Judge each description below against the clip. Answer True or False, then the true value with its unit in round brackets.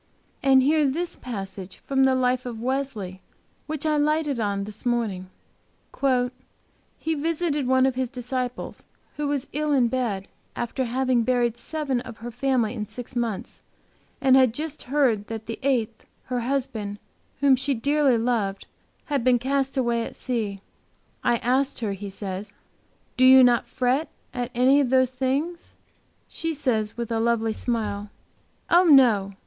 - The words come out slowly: False (155 wpm)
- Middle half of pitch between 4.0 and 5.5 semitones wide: False (3.3 semitones)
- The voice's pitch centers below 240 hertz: False (250 Hz)